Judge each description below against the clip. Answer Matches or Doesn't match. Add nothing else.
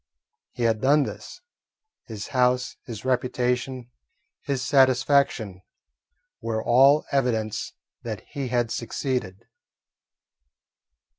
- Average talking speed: Doesn't match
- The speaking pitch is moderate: Doesn't match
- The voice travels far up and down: Doesn't match